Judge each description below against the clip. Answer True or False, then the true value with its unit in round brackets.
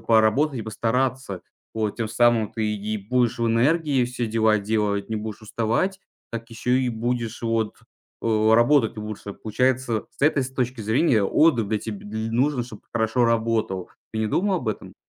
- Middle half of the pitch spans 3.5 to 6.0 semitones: False (2.5 semitones)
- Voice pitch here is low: True (115 Hz)